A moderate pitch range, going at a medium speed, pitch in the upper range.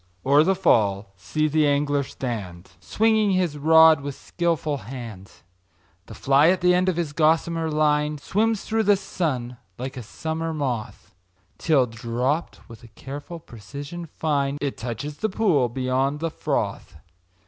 No: average, 4.5 semitones; average, 150 wpm; medium, 145 Hz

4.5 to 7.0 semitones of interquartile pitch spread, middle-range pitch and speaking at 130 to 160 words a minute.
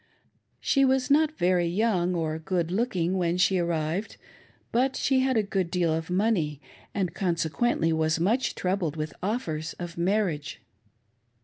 Yes: average, 4.8 semitones; medium, 180 Hz; average, 145 wpm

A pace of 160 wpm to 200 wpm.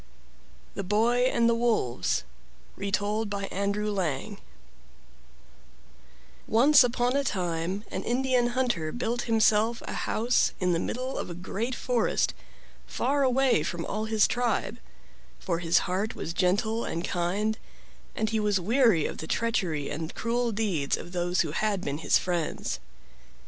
No: average, 145 wpm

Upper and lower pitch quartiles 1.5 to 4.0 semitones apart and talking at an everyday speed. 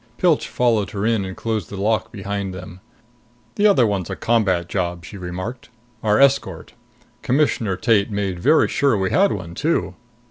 No: average, 4.4 semitones; average, 170 wpm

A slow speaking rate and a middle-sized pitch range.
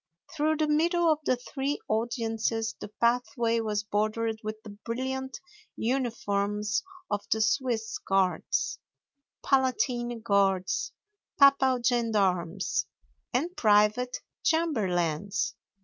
Yes: slow, 100 wpm; average, 4.1 semitones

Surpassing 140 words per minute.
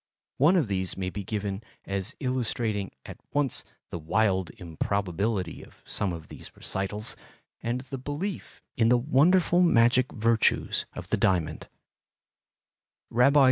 No: slow, 135 wpm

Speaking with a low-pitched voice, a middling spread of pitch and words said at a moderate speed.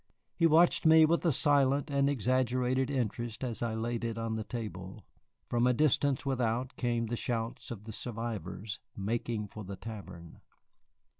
Yes: low, 120 Hz; average, 3.1 semitones; average, 160 wpm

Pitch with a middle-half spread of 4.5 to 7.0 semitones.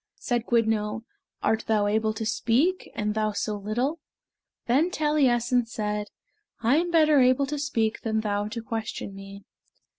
No: average, 4.0 semitones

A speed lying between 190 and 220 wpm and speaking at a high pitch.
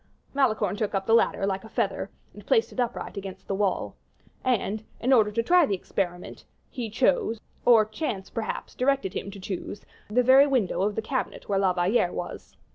Yes: average, 195 wpm; high, 215 Hz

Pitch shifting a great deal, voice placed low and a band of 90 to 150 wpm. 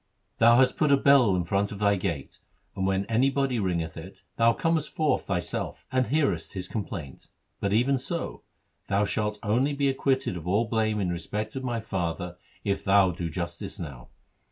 No: wide, 5.9 semitones; low, 105 Hz; average, 180 wpm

